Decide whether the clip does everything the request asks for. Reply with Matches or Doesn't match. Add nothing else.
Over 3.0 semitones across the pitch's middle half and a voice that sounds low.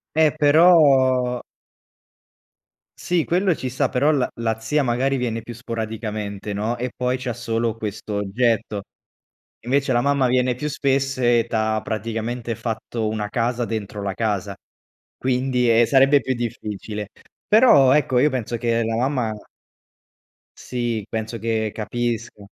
Doesn't match